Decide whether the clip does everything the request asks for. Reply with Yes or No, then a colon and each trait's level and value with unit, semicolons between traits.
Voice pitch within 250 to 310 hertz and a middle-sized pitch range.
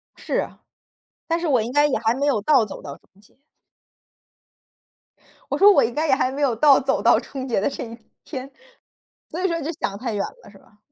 Yes: very high, 265 Hz; average, 4.7 semitones